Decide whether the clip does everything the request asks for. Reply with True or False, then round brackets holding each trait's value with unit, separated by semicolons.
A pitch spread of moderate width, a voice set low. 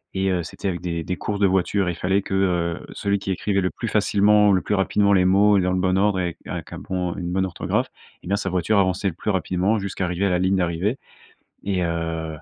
False (2.0 semitones; 95 Hz)